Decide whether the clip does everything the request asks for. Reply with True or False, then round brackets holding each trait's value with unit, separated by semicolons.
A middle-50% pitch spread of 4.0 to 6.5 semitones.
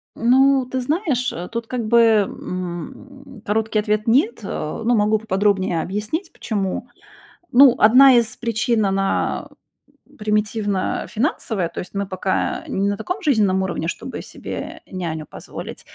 True (4.3 semitones)